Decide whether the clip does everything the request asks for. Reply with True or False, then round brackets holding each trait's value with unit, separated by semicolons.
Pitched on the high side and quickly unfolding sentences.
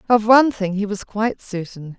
True (210 Hz; 210 wpm)